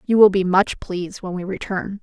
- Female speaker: Yes, female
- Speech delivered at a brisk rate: Yes, fast, 235 wpm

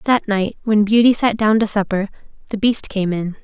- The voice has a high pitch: Yes, high, 210 Hz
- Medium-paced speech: No, fast, 210 wpm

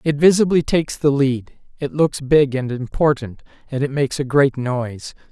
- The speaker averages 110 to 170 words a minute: No, average, 180 wpm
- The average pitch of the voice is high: No, medium, 140 Hz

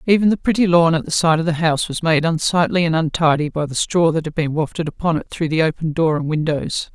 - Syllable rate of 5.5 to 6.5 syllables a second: Yes, 6.0 syllables/s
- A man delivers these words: No, female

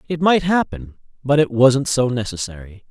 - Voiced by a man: Yes, male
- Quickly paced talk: No, average, 165 wpm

